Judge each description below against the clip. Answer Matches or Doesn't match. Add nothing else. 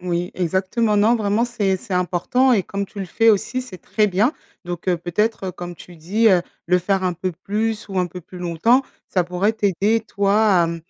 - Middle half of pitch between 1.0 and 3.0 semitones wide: Doesn't match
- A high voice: Matches